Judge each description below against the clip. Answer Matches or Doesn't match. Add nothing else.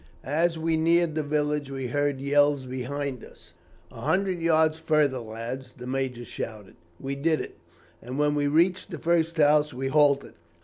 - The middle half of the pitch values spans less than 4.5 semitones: Matches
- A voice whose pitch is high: Doesn't match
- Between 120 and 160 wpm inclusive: Doesn't match